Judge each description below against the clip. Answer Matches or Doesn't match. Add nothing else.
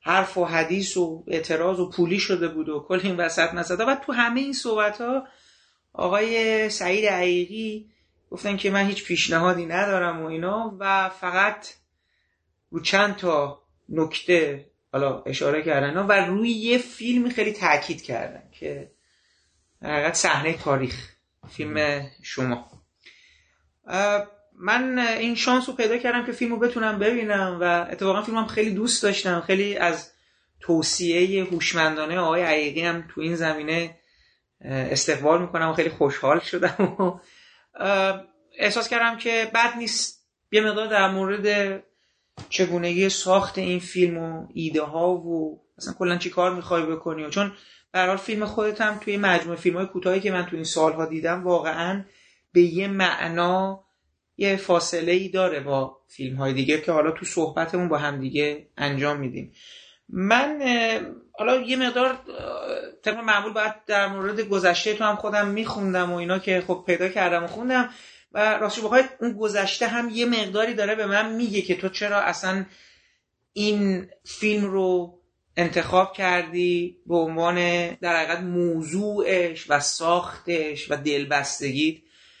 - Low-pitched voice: Doesn't match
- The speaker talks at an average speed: Matches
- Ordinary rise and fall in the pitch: Matches